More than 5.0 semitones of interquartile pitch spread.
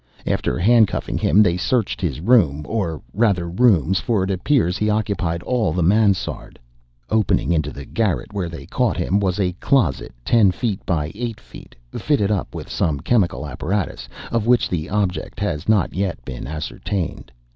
No: average, 4.3 semitones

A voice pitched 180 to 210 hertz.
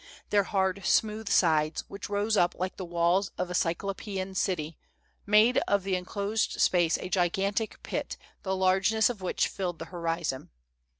Yes: high, 190 Hz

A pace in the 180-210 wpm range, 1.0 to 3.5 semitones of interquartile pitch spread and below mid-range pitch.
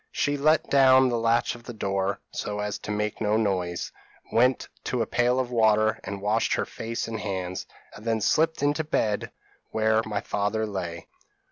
Yes: average, 190 wpm; average, 2.9 semitones; low, 110 Hz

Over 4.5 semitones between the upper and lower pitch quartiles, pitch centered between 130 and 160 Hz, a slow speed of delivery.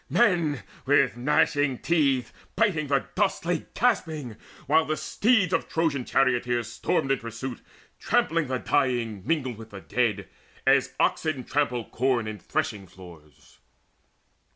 Yes: average, 5.1 semitones; low, 135 Hz; slow, 130 wpm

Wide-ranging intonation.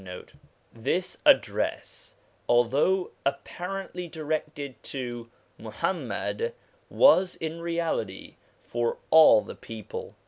Yes: wide, 6.6 semitones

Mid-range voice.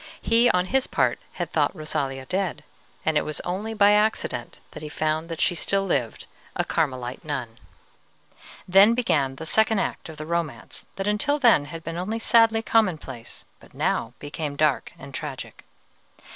Yes: medium, 165 Hz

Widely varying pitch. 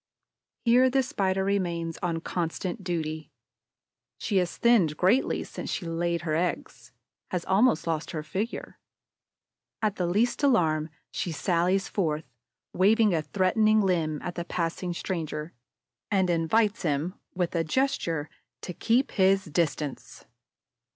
No: average, 3.5 semitones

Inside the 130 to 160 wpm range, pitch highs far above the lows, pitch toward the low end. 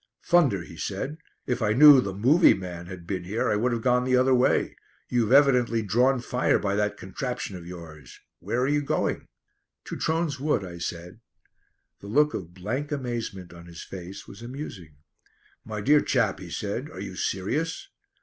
No: average, 180 wpm; wide, 6.0 semitones; low, 110 Hz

